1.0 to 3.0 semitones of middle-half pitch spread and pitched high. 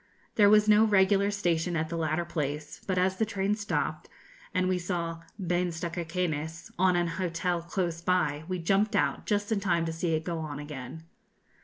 No: average, 2.7 semitones; medium, 175 Hz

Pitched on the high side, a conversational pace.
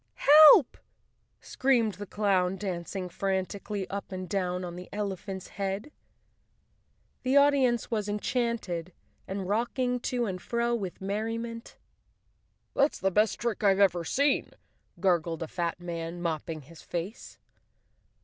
No: high, 200 Hz; slow, 130 wpm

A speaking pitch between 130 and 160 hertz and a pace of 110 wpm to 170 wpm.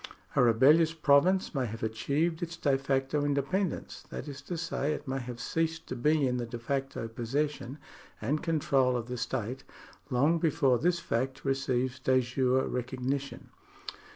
Yes: low, 135 Hz; average, 160 wpm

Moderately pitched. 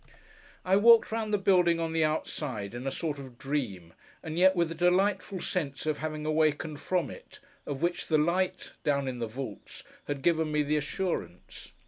Yes: medium, 155 Hz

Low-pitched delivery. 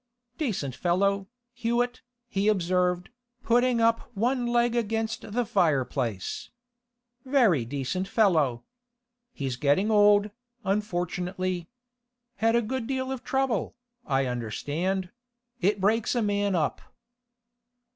No: high, 200 Hz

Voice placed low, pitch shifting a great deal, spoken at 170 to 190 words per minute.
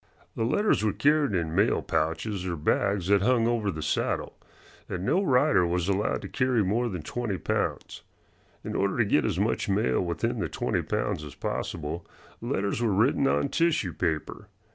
Yes: low, 100 Hz; wide, 5.8 semitones; average, 180 wpm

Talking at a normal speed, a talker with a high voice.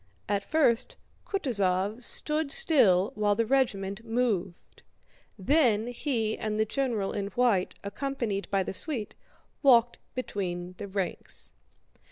No: slow, 120 wpm; high, 220 Hz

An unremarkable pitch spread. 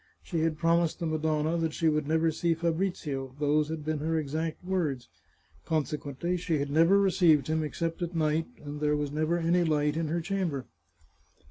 No: narrow, 1.9 semitones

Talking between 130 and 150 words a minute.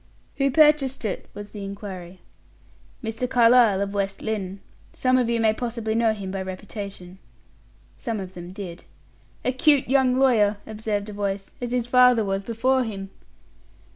No: average, 160 wpm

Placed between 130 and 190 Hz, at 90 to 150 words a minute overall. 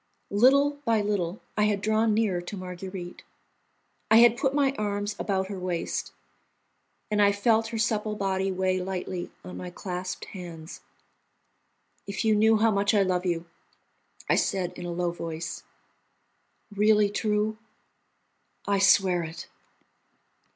No: high, 200 Hz; average, 140 wpm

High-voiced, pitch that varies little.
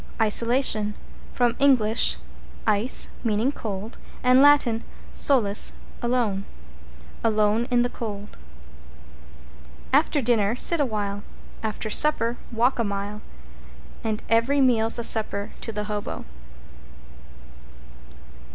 No: high, 225 Hz; average, 3.0 semitones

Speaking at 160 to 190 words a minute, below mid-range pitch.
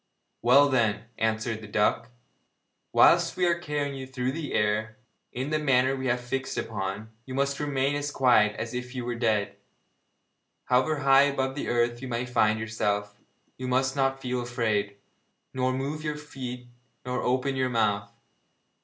Yes: average, 170 wpm; low, 125 Hz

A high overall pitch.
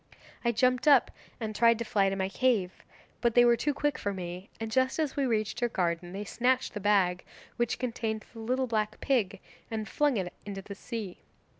Yes: high, 220 Hz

